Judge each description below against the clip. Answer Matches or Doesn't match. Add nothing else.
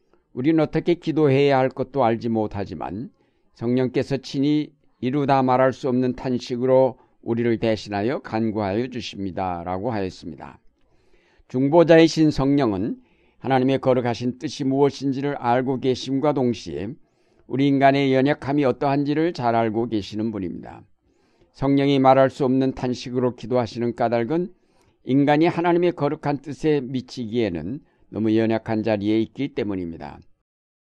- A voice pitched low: Matches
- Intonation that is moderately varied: Matches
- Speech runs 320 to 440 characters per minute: Matches